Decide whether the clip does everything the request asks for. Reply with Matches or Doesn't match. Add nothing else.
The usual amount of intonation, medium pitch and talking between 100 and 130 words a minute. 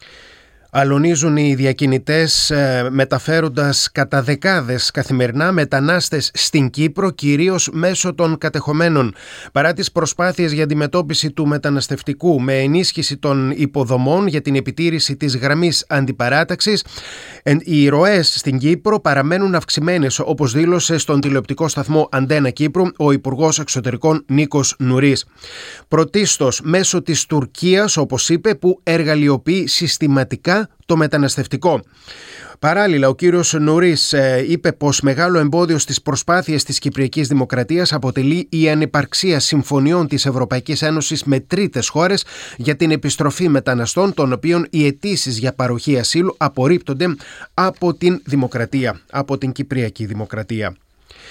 Matches